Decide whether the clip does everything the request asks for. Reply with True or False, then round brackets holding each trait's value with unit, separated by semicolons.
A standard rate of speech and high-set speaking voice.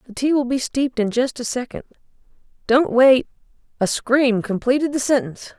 True (170 wpm; 255 Hz)